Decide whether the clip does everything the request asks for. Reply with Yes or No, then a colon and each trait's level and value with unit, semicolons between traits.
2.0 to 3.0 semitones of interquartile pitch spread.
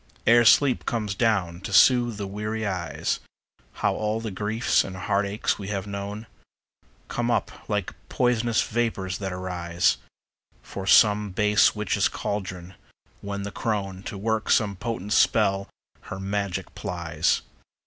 Yes: narrow, 2.4 semitones